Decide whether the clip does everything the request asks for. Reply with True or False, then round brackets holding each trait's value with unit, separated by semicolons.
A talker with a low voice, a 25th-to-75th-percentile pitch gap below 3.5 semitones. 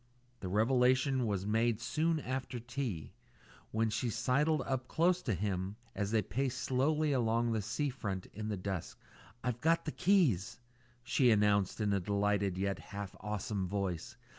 False (110 Hz; 4.4 semitones)